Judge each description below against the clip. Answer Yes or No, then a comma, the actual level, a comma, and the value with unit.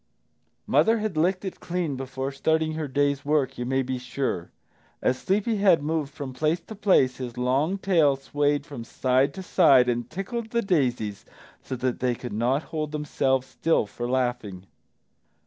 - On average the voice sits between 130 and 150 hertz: Yes, medium, 140 Hz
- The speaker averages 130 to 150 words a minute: No, average, 170 wpm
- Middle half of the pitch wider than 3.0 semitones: Yes, average, 4.4 semitones